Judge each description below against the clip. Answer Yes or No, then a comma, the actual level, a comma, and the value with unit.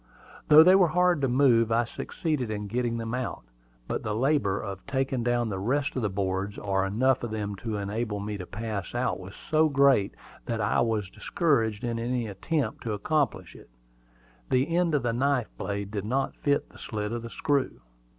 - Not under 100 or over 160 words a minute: No, average, 200 wpm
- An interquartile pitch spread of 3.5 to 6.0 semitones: Yes, average, 4.8 semitones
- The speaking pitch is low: Yes, low, 115 Hz